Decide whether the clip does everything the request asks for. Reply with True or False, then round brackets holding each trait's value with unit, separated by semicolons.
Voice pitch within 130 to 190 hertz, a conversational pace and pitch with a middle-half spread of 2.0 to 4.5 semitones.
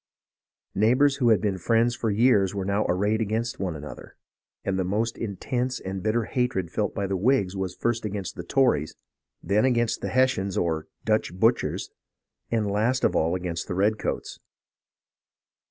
False (105 Hz; 170 wpm; 3.8 semitones)